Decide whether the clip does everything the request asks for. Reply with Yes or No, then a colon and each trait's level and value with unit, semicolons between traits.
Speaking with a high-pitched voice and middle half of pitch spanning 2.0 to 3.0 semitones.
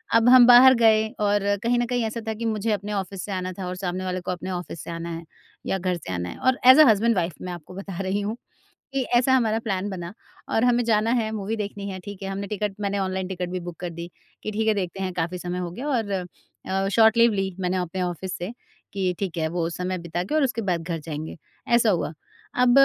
No: high, 195 Hz; average, 3.6 semitones